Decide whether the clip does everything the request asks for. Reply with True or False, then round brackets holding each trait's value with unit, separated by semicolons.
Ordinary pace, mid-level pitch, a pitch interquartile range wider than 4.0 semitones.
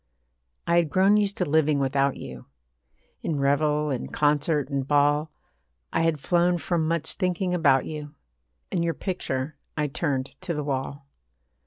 False (155 wpm; 150 Hz; 3.2 semitones)